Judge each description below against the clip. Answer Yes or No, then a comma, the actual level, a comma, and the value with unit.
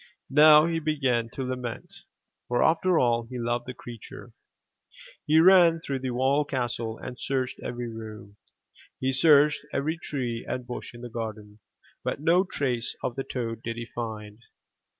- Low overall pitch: Yes, low, 125 Hz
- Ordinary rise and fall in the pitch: Yes, average, 4.0 semitones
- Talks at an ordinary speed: Yes, average, 160 wpm